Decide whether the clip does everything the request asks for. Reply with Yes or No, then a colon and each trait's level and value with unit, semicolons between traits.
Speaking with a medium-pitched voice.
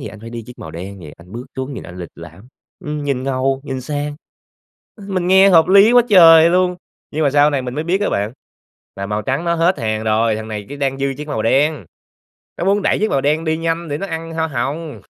Yes: medium, 145 Hz